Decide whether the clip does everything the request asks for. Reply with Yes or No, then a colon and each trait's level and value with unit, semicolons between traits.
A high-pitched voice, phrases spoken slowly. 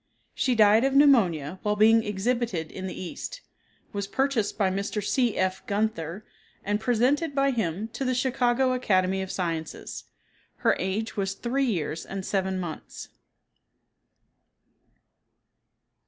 Yes: high, 210 Hz; slow, 130 wpm